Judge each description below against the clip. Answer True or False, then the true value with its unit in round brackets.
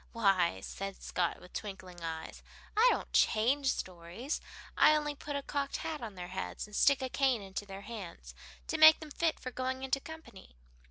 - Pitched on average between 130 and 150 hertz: False (230 Hz)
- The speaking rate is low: False (185 wpm)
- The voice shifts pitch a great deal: True (6.9 semitones)